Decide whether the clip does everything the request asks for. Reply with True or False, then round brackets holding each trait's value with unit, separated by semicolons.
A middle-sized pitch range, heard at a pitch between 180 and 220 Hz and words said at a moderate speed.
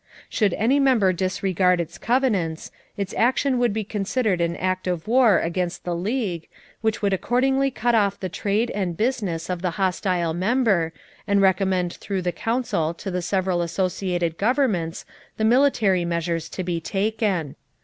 True (4.2 semitones; 190 Hz; 160 wpm)